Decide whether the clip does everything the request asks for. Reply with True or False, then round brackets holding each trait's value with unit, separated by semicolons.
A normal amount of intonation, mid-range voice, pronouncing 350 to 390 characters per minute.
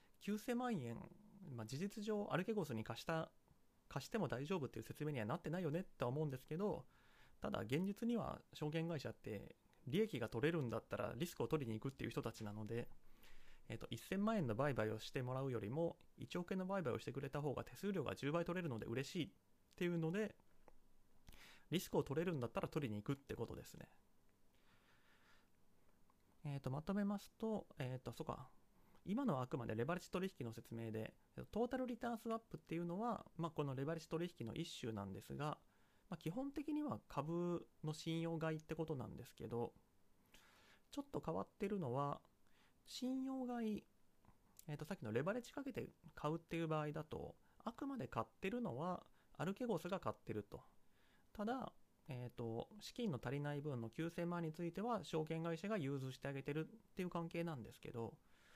False (7.7 semitones; 160 Hz; 375 characters per minute)